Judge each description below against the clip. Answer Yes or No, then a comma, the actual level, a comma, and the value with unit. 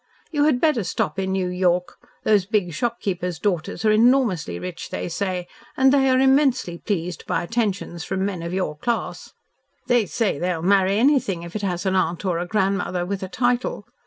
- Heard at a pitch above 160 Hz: Yes, high, 190 Hz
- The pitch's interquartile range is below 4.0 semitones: No, average, 4.7 semitones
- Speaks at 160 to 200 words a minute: Yes, average, 190 wpm